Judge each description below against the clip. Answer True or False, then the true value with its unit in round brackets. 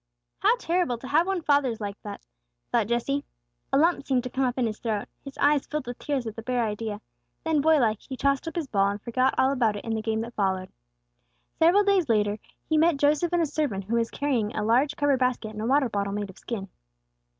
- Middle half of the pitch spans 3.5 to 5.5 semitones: True (5.0 semitones)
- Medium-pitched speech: False (250 Hz)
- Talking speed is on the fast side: True (240 wpm)